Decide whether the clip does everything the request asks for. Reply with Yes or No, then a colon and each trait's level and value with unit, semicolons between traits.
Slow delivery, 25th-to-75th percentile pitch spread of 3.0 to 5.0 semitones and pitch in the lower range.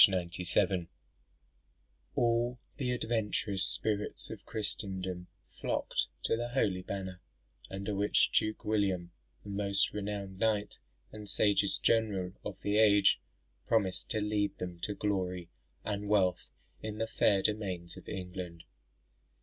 No: slow, 125 wpm; narrow, 2.5 semitones; low, 100 Hz